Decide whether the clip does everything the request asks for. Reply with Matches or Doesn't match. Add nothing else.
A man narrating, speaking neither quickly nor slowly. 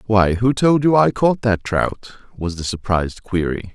Matches